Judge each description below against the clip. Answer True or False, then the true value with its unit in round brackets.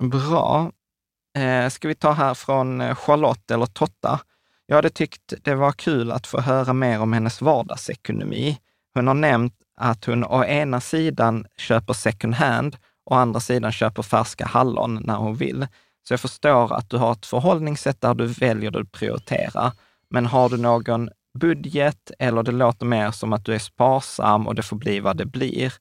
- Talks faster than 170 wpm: True (180 wpm)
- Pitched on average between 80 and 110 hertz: False (125 Hz)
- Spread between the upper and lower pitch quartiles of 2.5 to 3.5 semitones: True (3.1 semitones)